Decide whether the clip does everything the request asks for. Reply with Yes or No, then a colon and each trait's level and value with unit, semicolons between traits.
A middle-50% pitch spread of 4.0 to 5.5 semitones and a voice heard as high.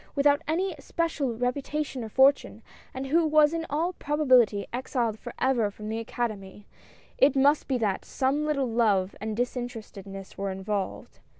Yes: average, 5.2 semitones; very high, 250 Hz